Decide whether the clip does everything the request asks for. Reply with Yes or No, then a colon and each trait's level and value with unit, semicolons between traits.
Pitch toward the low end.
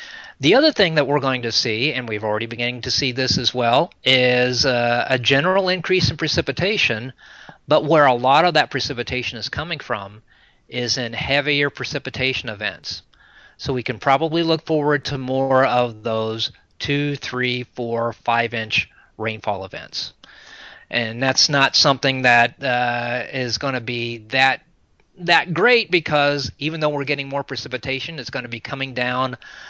Yes: low, 130 Hz